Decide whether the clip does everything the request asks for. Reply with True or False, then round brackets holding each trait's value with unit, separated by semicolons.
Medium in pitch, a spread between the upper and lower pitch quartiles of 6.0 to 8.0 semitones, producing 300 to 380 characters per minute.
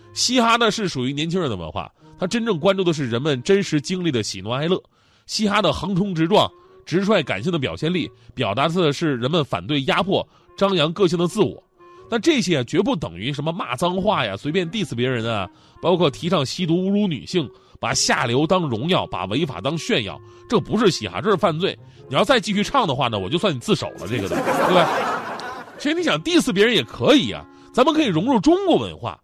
True (180 Hz; 7.0 semitones; 330 characters per minute)